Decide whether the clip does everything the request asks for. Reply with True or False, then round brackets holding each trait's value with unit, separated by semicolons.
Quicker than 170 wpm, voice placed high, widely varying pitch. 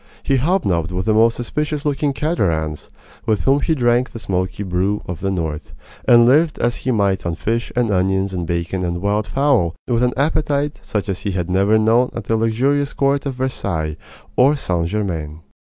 False (190 wpm; 110 Hz; 6.4 semitones)